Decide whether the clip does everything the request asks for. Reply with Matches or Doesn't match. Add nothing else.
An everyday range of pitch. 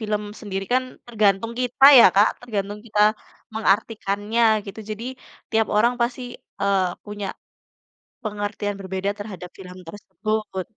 Doesn't match